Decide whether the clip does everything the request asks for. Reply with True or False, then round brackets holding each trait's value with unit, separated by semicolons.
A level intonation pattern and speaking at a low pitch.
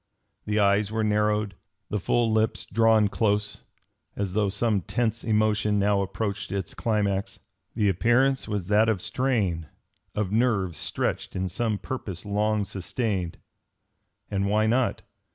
True (2.0 semitones; 105 Hz)